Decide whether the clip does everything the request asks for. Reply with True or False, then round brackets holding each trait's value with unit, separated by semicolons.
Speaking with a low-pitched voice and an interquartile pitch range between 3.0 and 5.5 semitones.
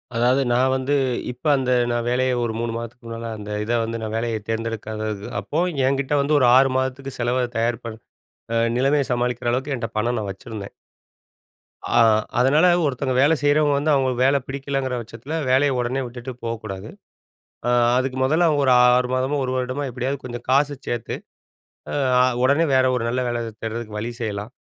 False (125 Hz; 2.6 semitones)